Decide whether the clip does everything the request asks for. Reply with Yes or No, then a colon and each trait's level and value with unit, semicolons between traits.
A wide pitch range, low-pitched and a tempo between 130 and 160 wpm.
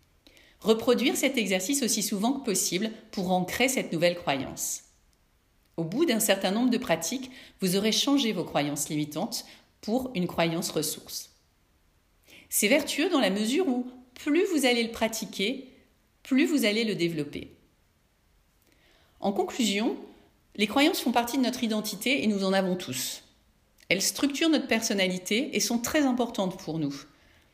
No: wide, 7.0 semitones; high, 215 Hz; average, 150 wpm